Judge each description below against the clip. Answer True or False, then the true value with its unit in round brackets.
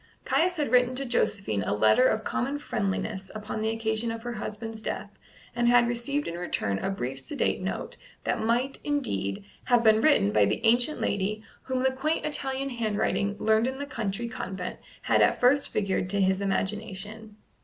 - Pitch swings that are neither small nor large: True (4.3 semitones)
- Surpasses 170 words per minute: True (180 wpm)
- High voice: True (220 Hz)